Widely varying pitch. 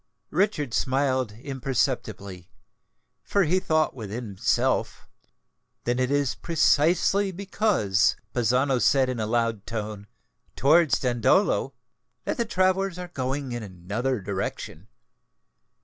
Yes: wide, 6.9 semitones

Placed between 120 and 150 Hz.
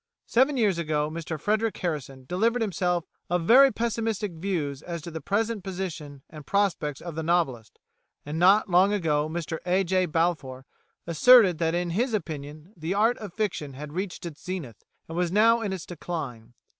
No: medium, 175 Hz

